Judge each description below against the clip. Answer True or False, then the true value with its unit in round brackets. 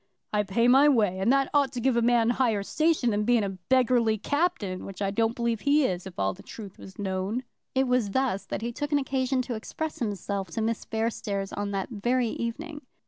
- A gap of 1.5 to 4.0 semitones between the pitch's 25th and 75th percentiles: False (4.5 semitones)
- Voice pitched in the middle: False (230 Hz)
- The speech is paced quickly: True (220 wpm)